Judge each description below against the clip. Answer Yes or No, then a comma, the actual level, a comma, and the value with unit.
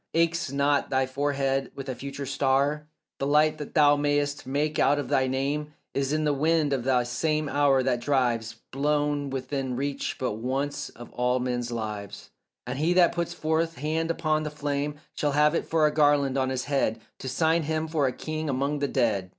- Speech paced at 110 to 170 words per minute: No, average, 200 wpm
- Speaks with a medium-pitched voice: Yes, medium, 145 Hz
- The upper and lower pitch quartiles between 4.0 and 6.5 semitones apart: No, narrow, 2.4 semitones